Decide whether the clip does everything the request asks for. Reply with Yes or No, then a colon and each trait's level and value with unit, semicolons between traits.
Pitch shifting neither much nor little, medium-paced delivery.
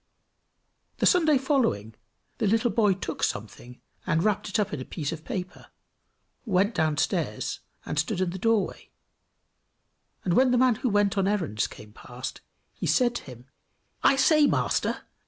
No: wide, 7.8 semitones; average, 160 wpm